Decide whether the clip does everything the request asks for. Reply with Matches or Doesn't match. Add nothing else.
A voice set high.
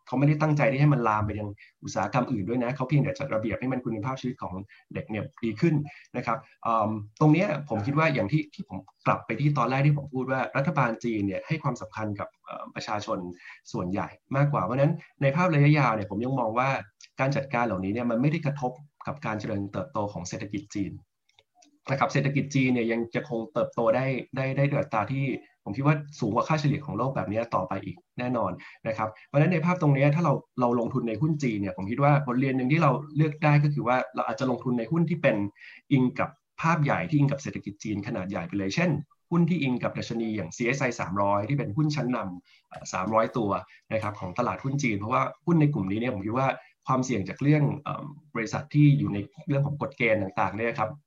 Doesn't match